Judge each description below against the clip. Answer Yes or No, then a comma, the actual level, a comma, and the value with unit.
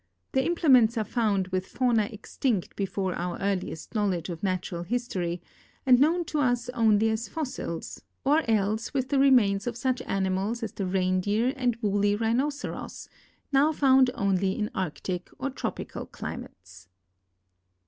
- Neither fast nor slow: Yes, average, 150 wpm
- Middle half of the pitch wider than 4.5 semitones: Yes, average, 5.2 semitones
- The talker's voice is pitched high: Yes, high, 215 Hz